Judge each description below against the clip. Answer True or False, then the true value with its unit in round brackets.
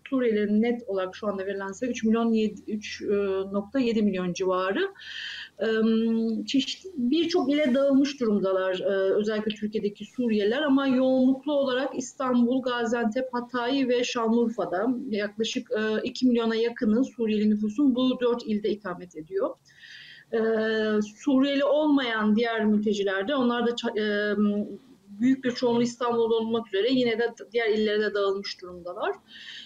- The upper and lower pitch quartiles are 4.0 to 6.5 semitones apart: False (3.3 semitones)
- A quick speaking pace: False (115 wpm)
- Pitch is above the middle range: True (230 Hz)